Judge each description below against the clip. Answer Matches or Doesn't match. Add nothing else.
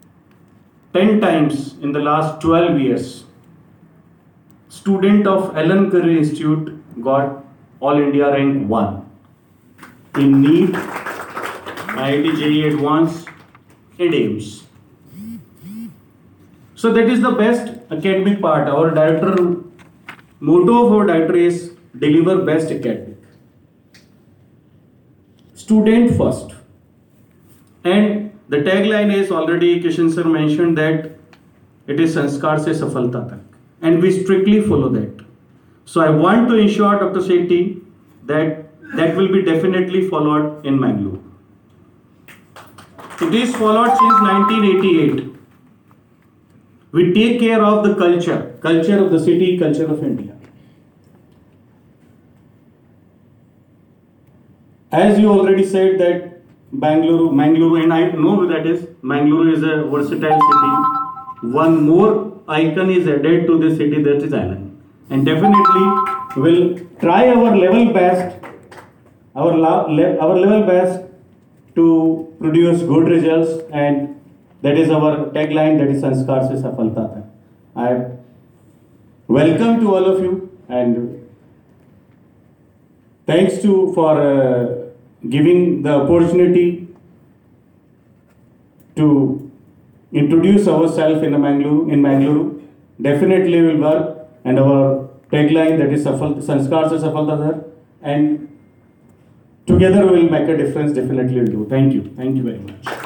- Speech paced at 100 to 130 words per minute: Matches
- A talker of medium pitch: Matches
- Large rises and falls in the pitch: Doesn't match